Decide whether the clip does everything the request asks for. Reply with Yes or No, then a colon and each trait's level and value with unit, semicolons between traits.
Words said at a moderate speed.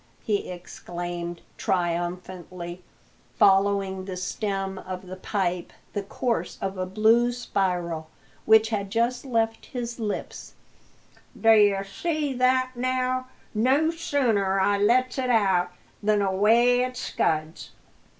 No: slow, 120 wpm